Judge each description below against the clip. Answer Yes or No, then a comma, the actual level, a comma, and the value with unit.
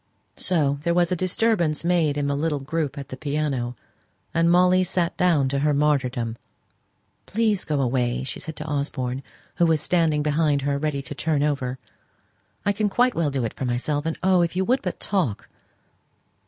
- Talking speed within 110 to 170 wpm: No, average, 185 wpm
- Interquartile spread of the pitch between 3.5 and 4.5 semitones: Yes, average, 3.8 semitones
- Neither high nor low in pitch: Yes, medium, 150 Hz